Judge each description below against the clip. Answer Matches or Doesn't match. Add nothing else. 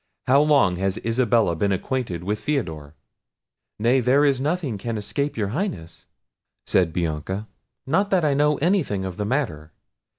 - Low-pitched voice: Matches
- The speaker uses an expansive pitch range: Matches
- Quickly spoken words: Doesn't match